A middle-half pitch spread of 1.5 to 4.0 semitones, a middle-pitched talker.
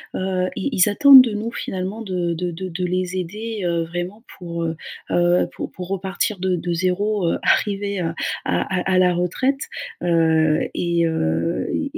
Yes: average, 2.8 semitones; medium, 180 Hz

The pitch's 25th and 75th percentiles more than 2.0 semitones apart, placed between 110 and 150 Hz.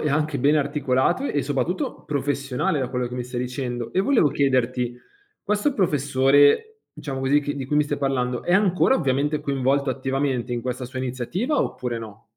Yes: average, 2.7 semitones; low, 135 Hz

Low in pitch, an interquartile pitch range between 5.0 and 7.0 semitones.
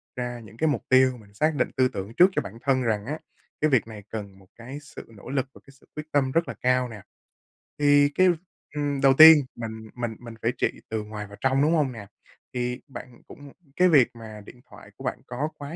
No: low, 125 Hz; average, 4.3 semitones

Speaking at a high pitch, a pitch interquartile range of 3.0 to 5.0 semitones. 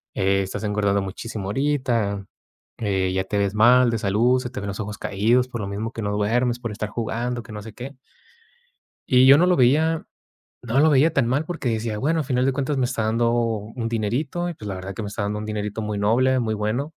No: low, 115 Hz; average, 3.7 semitones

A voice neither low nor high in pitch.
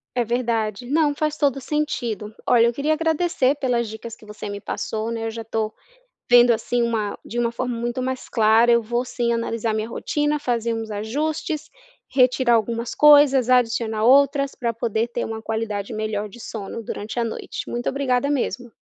No: high, 235 Hz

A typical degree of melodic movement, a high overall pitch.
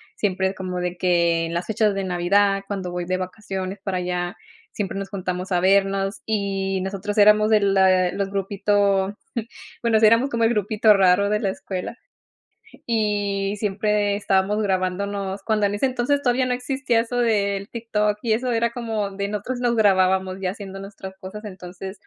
No: narrow, 2.0 semitones; high, 200 Hz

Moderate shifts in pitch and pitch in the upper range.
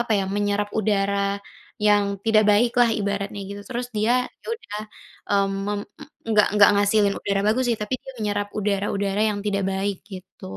No: narrow, 1.1 semitones; high, 205 Hz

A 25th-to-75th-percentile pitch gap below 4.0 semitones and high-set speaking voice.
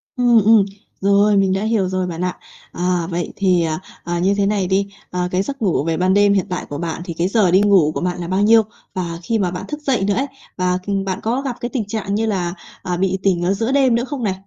Yes: average, 3.2 semitones; high, 195 Hz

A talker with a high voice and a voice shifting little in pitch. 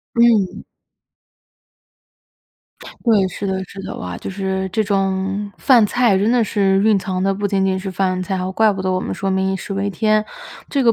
Yes: high, 195 Hz; narrow, 1.9 semitones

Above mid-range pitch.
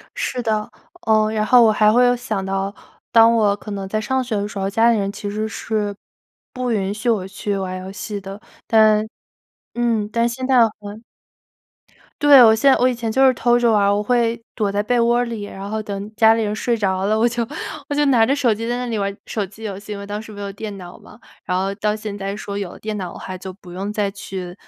Yes: high, 215 Hz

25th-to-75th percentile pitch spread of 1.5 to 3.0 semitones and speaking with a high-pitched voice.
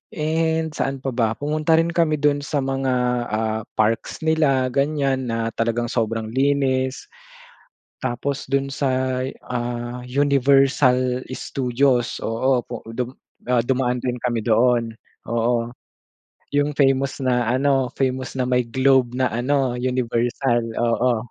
No: narrow, 2.4 semitones; low, 130 Hz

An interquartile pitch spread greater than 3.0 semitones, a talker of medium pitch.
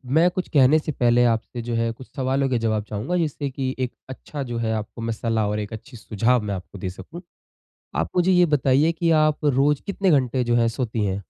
No: average, 4.7 semitones; low, 125 Hz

